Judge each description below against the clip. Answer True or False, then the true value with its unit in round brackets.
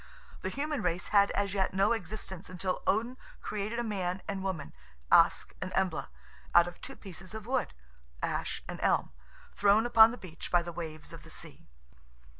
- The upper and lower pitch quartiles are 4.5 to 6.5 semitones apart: False (3.6 semitones)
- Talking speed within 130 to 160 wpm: False (180 wpm)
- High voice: True (195 Hz)